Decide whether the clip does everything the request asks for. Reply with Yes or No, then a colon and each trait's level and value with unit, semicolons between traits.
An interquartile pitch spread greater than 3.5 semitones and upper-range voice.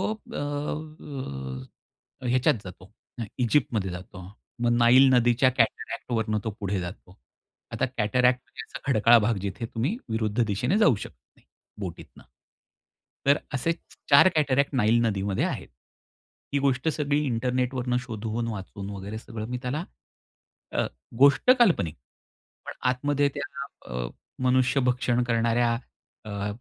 No: average, 4.3 semitones; low, 120 Hz